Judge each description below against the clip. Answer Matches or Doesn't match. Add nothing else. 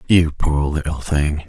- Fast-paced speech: Doesn't match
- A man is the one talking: Matches